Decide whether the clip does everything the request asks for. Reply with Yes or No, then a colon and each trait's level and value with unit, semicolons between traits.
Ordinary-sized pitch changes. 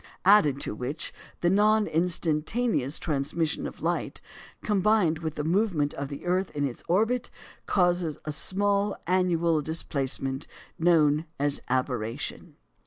Yes: average, 4.8 semitones